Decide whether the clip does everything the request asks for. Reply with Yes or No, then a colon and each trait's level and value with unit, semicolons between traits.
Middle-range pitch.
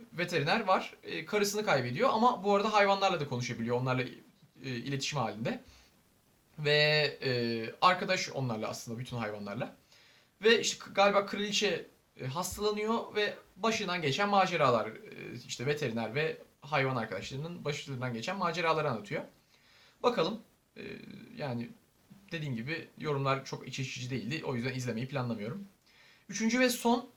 Yes: medium, 150 Hz